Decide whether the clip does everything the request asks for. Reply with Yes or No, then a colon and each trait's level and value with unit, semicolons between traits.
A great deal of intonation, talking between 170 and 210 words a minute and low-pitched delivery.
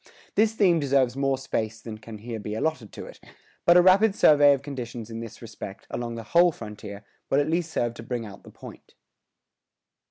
Yes: wide, 5.7 semitones; average, 200 wpm; low, 120 Hz